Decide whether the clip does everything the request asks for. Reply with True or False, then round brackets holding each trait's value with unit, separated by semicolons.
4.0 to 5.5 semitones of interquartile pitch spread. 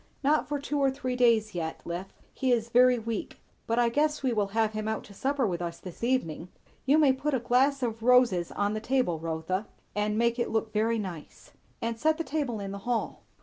True (4.3 semitones)